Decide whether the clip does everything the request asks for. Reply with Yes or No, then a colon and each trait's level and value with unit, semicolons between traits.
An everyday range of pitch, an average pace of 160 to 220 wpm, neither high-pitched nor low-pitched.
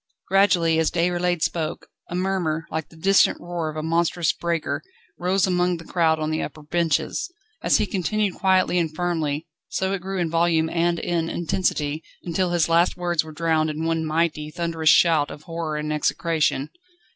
No: narrow, 1.9 semitones; average, 180 wpm; medium, 165 Hz